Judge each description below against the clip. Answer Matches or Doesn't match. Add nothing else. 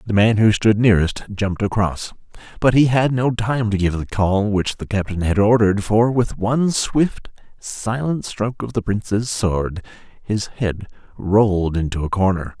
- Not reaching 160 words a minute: Doesn't match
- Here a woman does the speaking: Doesn't match